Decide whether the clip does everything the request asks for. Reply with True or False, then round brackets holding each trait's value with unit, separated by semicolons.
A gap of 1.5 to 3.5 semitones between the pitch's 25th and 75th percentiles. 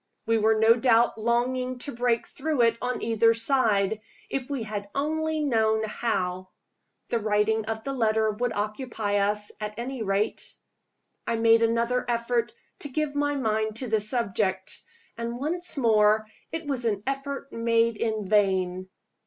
True (2.8 semitones)